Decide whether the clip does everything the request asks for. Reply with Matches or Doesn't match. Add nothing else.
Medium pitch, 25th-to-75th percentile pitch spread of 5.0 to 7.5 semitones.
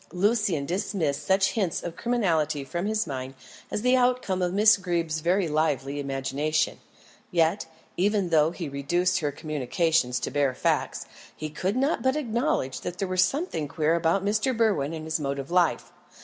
Matches